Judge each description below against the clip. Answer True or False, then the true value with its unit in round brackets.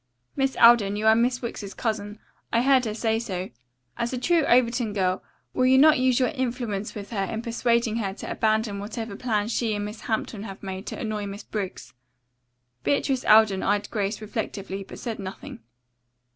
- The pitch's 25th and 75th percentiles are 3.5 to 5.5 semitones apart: False (2.8 semitones)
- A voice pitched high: True (220 Hz)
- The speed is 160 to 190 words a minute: True (185 wpm)